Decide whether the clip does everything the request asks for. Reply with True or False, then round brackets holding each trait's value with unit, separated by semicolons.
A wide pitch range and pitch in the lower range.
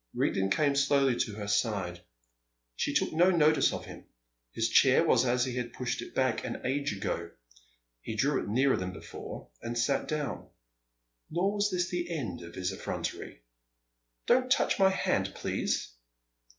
True (7.3 semitones; 130 Hz)